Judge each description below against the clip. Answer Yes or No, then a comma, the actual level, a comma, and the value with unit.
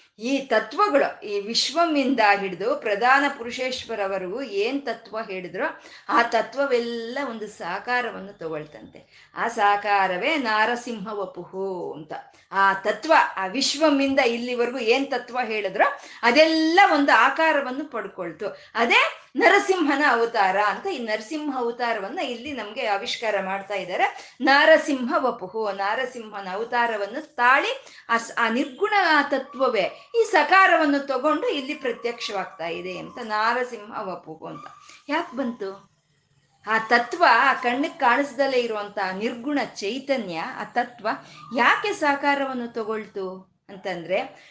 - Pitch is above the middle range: Yes, high, 235 Hz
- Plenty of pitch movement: Yes, wide, 5.9 semitones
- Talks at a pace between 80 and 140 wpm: Yes, fast, 105 wpm